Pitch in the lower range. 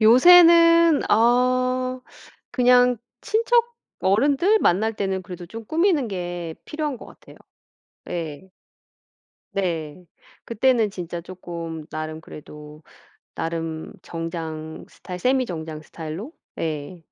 No: high, 190 Hz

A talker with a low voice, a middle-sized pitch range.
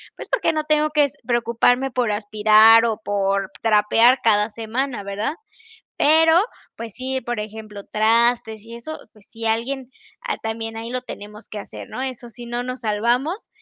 No: high, 230 Hz; average, 3.0 semitones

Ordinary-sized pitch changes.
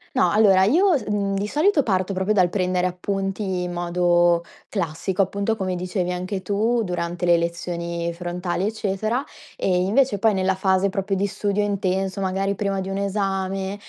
No: narrow, 2.1 semitones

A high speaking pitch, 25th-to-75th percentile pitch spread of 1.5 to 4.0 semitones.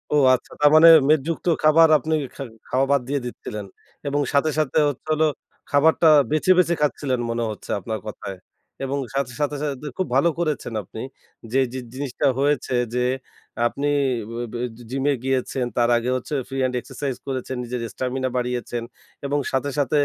No: low, 135 Hz; average, 2.9 semitones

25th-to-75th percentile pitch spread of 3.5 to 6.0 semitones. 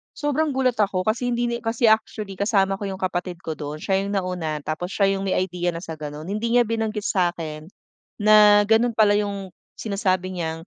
Yes: average, 3.8 semitones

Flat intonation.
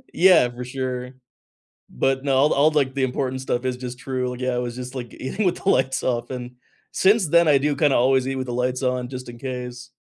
Yes: narrow, 1.5 semitones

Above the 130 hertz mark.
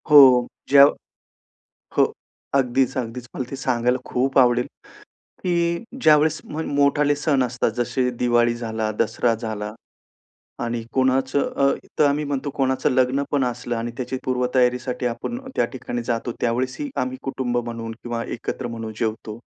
No: low, 125 Hz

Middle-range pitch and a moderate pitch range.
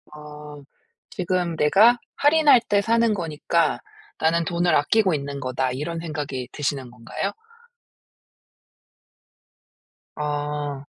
Yes: medium, 155 Hz; average, 4.1 semitones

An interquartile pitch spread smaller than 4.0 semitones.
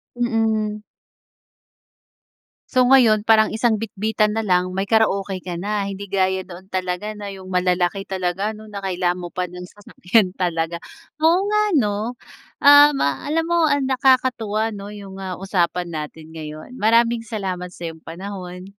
Yes: average, 3.6 semitones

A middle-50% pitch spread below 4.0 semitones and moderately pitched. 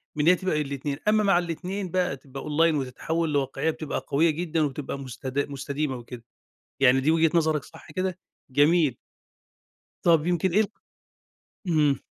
Yes: average, 3.4 semitones; medium, 155 Hz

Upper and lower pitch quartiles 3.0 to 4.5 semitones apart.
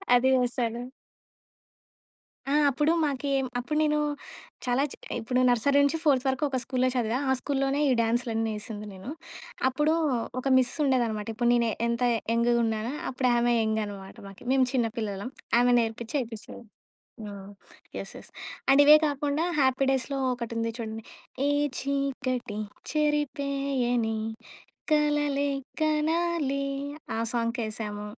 Yes: average, 3.5 semitones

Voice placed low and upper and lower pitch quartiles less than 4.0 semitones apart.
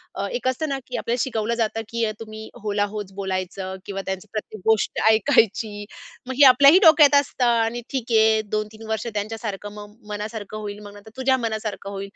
No: high, 220 Hz; narrow, 2.4 semitones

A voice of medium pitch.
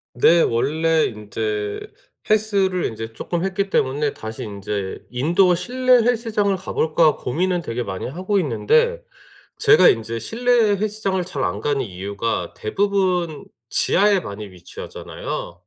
Yes: medium, 165 Hz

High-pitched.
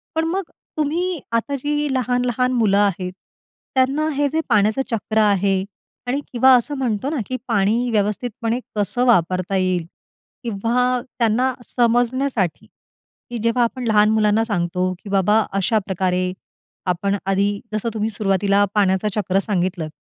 Yes: high, 220 Hz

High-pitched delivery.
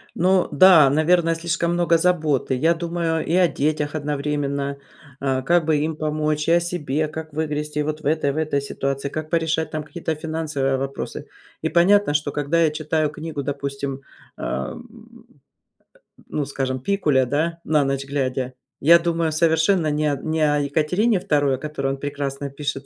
No: medium, 150 Hz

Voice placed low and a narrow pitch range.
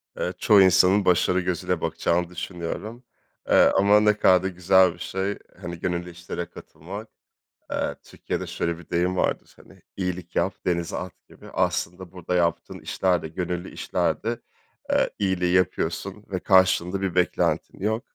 Yes: very low, 90 Hz; narrow, 1.6 semitones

